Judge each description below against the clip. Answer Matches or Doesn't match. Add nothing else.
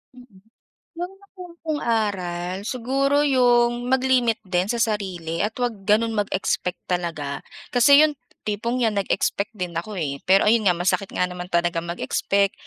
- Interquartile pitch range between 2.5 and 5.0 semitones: Doesn't match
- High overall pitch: Matches